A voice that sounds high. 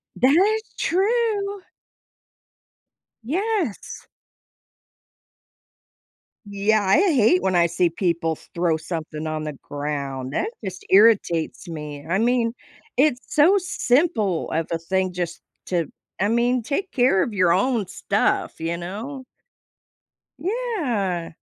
Yes: high, 200 Hz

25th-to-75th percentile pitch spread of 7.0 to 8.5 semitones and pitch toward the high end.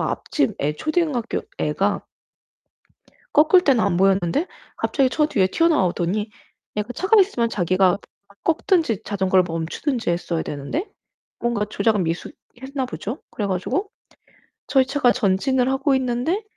Yes: wide, 7.4 semitones; high, 240 Hz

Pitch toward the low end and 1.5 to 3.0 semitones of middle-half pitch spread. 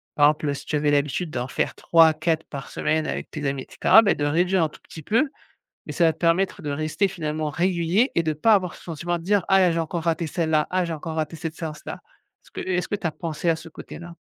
No: medium, 165 Hz; narrow, 2.6 semitones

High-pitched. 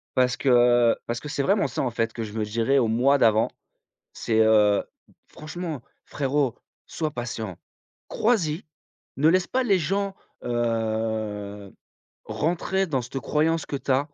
No: low, 125 Hz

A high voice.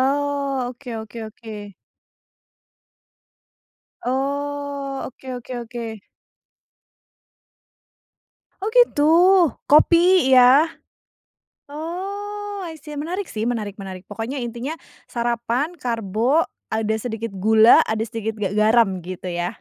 Yes: high, 245 Hz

